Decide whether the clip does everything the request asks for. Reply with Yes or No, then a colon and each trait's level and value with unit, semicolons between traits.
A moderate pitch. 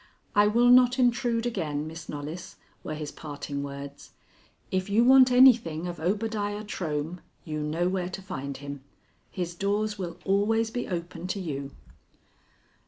Yes: medium, 180 Hz